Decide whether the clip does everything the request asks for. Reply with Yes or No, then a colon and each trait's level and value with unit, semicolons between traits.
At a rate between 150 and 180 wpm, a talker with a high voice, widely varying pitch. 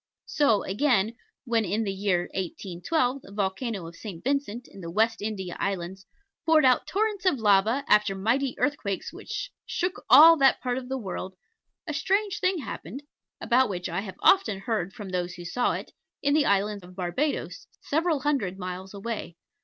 Yes: average, 175 wpm; high, 215 Hz; wide, 6.6 semitones